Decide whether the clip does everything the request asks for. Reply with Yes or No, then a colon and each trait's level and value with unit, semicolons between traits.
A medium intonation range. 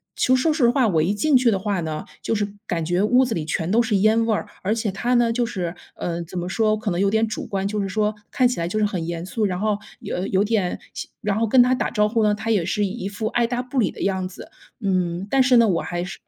Yes: average, 3.7 semitones